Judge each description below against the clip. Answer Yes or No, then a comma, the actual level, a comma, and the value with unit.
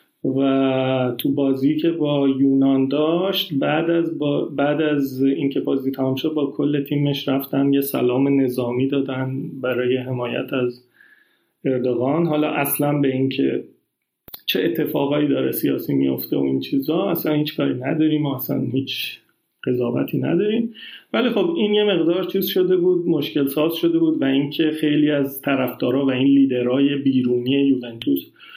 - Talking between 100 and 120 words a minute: No, average, 145 wpm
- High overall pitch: No, medium, 140 Hz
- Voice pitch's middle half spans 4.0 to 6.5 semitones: No, narrow, 2.5 semitones